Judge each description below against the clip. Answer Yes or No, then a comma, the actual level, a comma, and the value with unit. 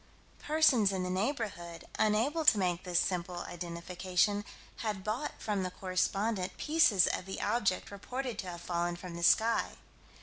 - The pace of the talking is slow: No, average, 155 wpm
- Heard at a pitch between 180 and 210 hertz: Yes, high, 190 Hz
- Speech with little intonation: No, average, 3.7 semitones